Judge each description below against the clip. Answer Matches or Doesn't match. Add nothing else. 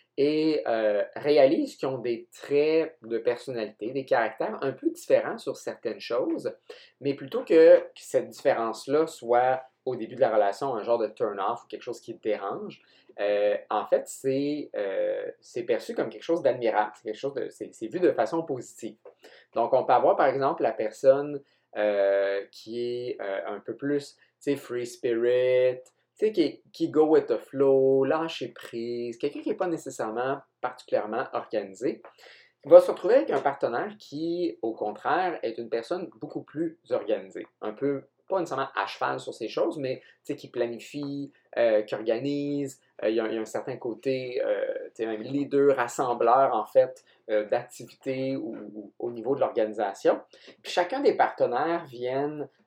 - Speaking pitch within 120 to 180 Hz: Matches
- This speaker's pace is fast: Doesn't match